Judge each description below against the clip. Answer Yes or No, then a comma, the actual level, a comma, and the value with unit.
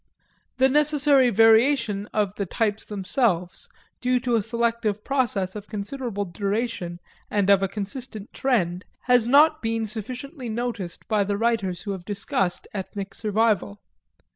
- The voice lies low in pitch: No, high, 215 Hz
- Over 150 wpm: No, average, 140 wpm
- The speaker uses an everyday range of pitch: Yes, average, 3.8 semitones